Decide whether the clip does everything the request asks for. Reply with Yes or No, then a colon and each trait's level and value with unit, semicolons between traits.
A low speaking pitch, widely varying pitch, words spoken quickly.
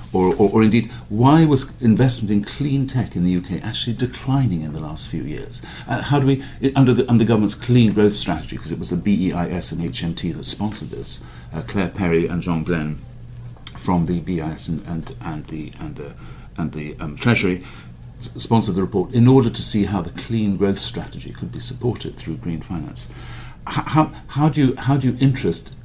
Yes: low, 110 Hz; wide, 6.1 semitones; fast, 210 wpm